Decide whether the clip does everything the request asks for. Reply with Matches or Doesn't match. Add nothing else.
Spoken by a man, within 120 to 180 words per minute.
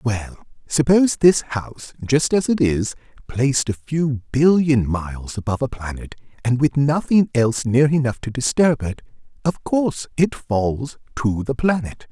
Matches